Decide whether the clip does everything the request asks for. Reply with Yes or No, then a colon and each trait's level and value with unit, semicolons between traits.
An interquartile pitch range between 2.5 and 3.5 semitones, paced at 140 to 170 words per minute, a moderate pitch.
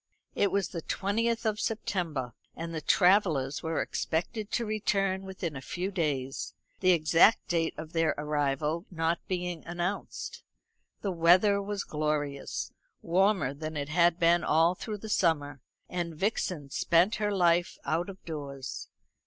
No: average, 4.1 semitones; average, 145 wpm; medium, 170 Hz